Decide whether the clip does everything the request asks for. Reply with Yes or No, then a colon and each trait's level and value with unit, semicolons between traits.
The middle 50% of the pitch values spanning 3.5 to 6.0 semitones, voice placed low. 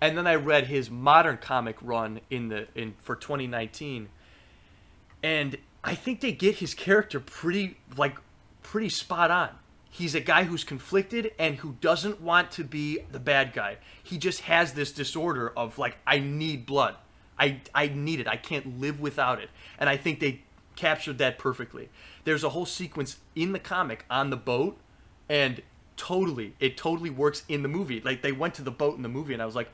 No: average, 4.8 semitones; medium, 145 Hz